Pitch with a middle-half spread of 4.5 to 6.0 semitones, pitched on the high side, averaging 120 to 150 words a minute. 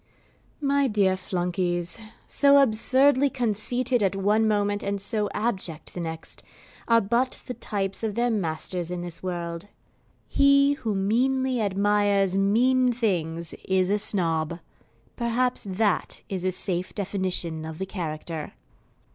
Yes: average, 4.8 semitones; high, 200 Hz; slow, 135 wpm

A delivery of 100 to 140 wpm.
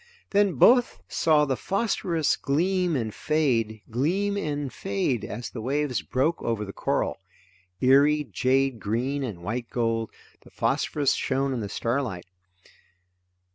Yes: slow, 135 wpm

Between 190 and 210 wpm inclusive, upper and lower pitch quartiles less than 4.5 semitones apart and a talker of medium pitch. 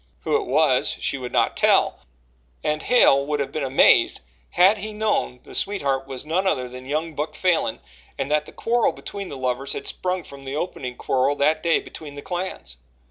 No: average, 195 wpm; average, 5.1 semitones; medium, 150 Hz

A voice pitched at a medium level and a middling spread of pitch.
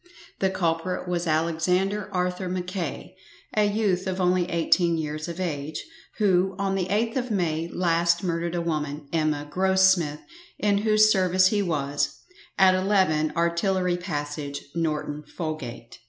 Yes: medium, 175 Hz; average, 3.1 semitones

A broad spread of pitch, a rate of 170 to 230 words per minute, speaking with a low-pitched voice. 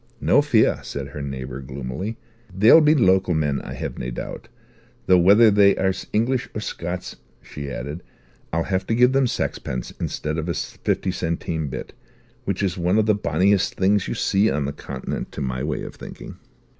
Yes: wide, 6.2 semitones; average, 185 wpm; very low, 90 Hz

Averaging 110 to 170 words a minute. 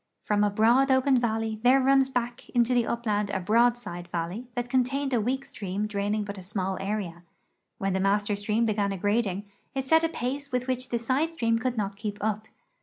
No: fast, 205 wpm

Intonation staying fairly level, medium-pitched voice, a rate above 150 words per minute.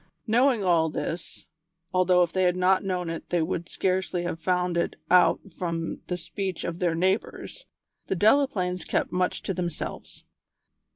Yes: narrow, 1.6 semitones; medium, 180 Hz; average, 160 wpm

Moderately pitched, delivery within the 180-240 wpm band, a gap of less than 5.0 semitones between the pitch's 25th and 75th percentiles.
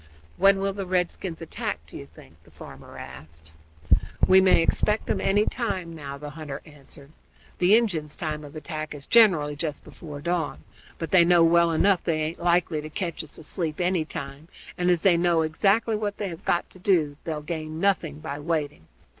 Yes: medium, 165 Hz; average, 190 wpm; average, 3.4 semitones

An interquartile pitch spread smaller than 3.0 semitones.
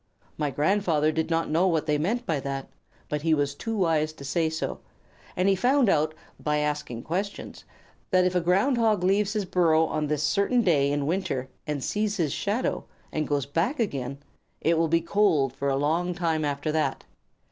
No: average, 4.4 semitones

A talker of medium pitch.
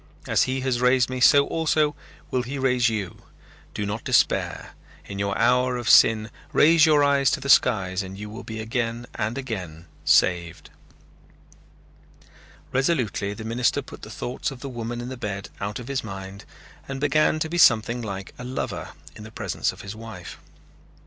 No: low, 120 Hz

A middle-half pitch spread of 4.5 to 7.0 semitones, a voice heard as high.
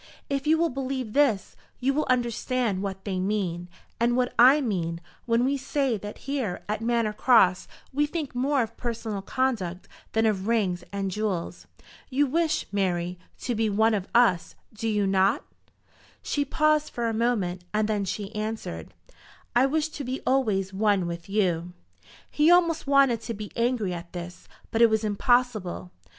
Yes: average, 5.0 semitones; high, 220 Hz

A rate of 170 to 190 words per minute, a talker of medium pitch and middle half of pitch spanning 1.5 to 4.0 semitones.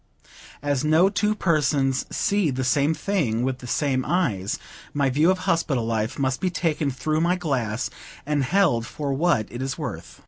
No: average, 175 wpm; medium, 145 Hz; average, 4.8 semitones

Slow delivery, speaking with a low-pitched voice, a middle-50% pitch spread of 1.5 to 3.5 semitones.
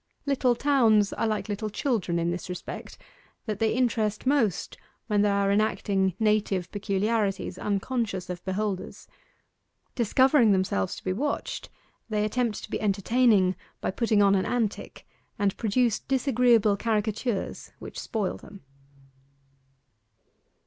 No: slow, 130 wpm; high, 210 Hz; average, 3.0 semitones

